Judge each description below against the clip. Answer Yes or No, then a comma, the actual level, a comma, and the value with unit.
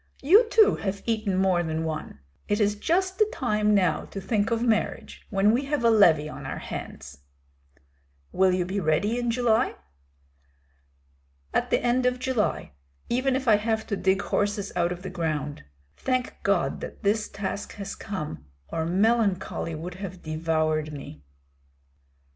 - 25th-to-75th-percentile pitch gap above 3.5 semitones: Yes, average, 5.2 semitones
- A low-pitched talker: No, high, 200 Hz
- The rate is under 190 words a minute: Yes, average, 160 wpm